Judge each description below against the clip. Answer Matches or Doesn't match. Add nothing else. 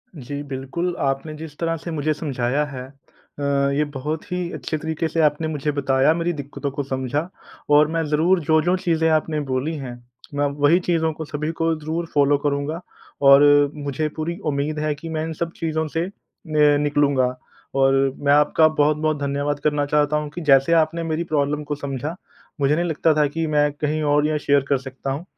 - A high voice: Doesn't match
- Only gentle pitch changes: Matches